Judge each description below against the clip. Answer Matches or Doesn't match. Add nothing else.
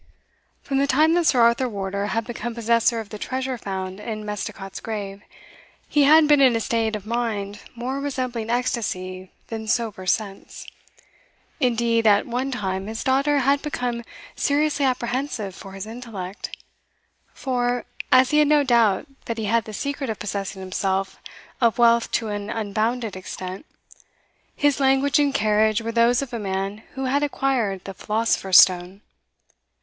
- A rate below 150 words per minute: Doesn't match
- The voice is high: Matches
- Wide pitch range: Doesn't match